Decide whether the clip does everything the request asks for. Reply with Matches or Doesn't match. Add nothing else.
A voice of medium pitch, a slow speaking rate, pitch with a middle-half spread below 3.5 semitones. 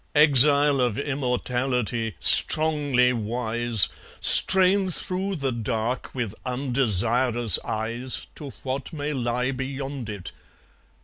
Doesn't match